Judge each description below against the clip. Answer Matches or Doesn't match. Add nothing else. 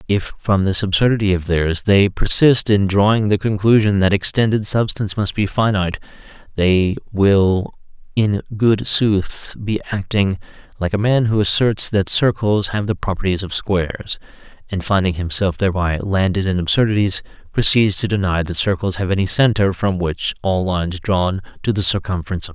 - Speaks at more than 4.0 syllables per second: Matches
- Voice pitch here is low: Matches